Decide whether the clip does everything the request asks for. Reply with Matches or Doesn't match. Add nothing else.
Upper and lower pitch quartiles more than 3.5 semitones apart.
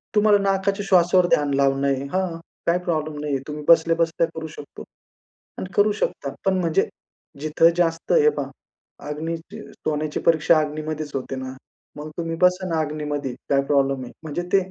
Doesn't match